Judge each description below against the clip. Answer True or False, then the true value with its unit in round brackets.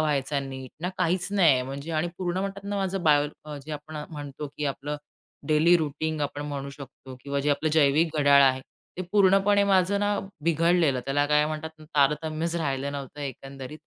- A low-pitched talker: False (150 Hz)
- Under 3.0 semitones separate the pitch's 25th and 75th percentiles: False (3.3 semitones)